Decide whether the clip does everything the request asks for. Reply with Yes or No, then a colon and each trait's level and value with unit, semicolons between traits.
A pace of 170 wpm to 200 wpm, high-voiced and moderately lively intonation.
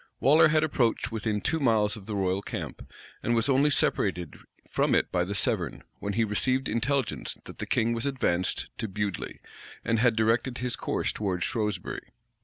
No: average, 180 wpm; low, 115 Hz; average, 3.8 semitones